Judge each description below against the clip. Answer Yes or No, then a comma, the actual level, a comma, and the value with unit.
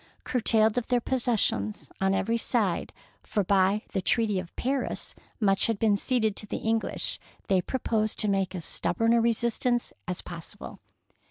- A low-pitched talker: No, high, 215 Hz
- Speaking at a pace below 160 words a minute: No, average, 170 wpm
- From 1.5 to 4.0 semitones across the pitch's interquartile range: Yes, average, 3.3 semitones